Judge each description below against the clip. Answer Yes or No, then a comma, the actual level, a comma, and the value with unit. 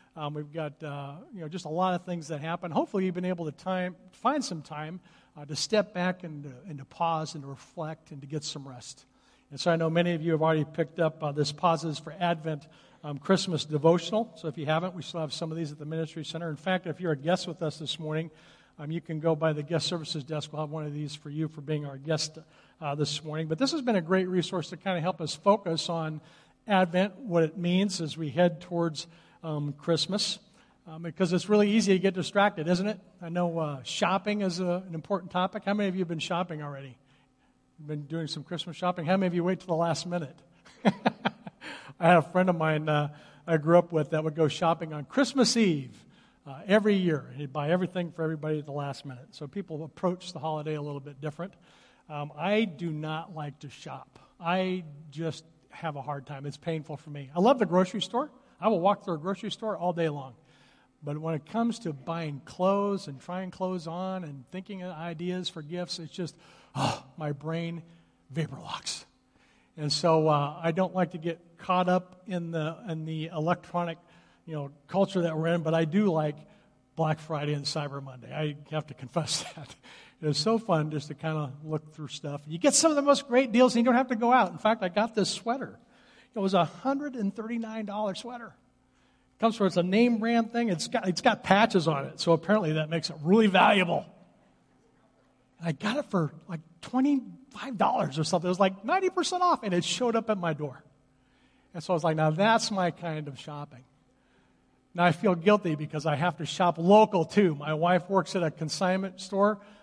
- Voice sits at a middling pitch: Yes, medium, 170 Hz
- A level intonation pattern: No, average, 3.5 semitones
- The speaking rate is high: Yes, fast, 225 wpm